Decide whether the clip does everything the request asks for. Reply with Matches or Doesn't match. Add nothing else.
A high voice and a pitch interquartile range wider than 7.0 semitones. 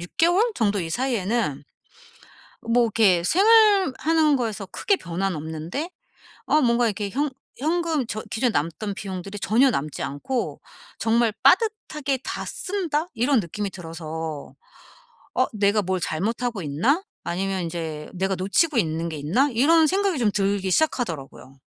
Matches